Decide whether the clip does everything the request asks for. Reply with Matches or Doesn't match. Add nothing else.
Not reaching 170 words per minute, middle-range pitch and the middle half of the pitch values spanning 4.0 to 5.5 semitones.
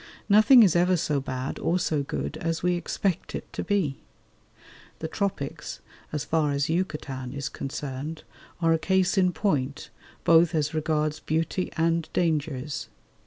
Doesn't match